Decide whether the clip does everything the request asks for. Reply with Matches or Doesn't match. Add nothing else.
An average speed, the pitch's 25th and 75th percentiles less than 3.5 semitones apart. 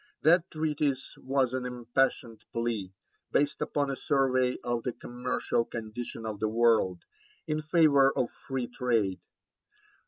Doesn't match